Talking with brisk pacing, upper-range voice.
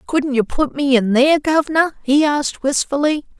No: average, 175 wpm; very high, 285 Hz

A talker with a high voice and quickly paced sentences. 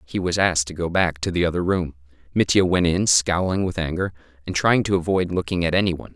No: very low, 85 Hz; fast, 235 wpm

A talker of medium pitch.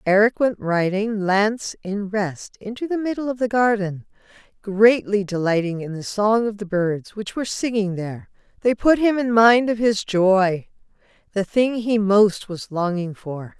No: high, 205 Hz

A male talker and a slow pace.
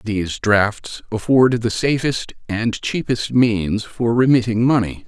Yes: male; slow, 130 wpm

